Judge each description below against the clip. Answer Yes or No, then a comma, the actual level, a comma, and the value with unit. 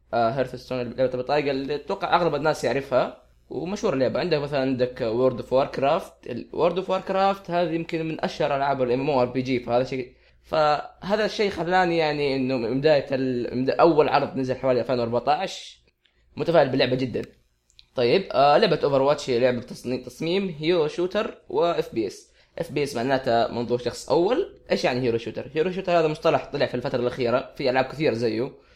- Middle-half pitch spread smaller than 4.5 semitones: No, wide, 5.4 semitones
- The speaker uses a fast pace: Yes, fast, 185 wpm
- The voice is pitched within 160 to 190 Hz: No, medium, 140 Hz